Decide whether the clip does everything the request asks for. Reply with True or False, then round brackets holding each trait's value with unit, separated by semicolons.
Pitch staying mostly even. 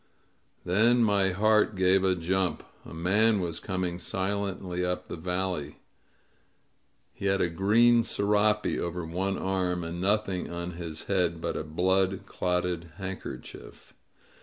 True (2.3 semitones)